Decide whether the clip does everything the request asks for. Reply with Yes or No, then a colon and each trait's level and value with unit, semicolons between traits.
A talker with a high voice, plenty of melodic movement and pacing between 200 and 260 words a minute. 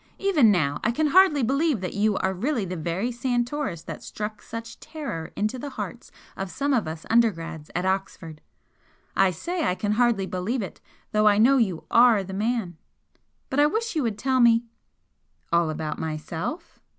No: high, 215 Hz; wide, 6.3 semitones; average, 185 wpm